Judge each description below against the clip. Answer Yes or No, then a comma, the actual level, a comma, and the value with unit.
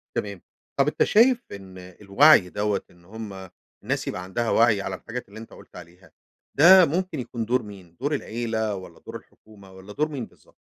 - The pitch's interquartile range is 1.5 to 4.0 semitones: No, average, 5.3 semitones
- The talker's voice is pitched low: Yes, low, 110 Hz